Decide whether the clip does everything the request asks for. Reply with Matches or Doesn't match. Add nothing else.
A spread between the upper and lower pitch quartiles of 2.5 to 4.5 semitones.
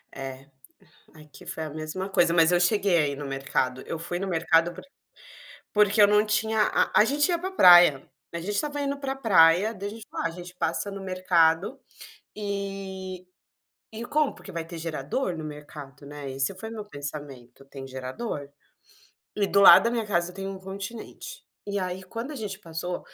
Doesn't match